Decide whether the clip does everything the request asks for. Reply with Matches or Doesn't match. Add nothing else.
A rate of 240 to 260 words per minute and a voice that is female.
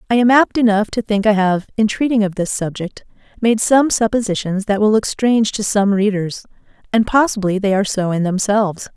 Doesn't match